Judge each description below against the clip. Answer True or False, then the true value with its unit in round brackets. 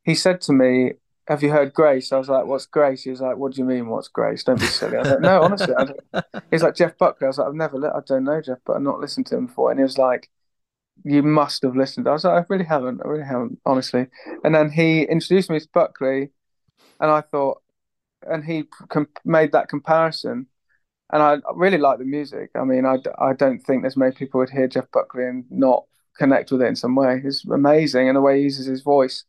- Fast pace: True (250 wpm)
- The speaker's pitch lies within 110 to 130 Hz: False (140 Hz)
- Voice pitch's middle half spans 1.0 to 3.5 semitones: True (3.0 semitones)